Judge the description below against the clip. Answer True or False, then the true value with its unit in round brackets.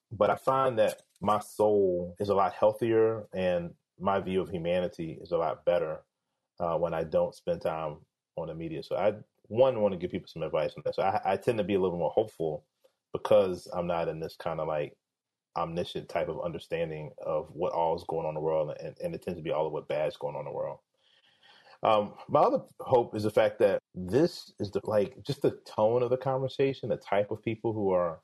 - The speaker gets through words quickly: True (235 wpm)